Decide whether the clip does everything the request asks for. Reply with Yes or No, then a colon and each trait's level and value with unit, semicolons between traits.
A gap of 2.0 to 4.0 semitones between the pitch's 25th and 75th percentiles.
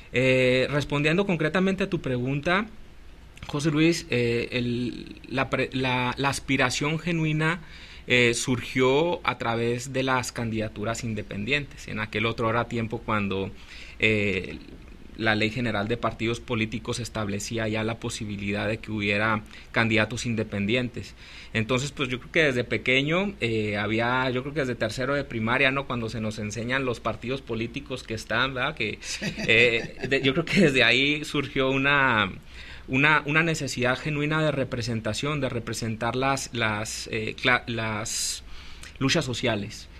Yes: average, 3.6 semitones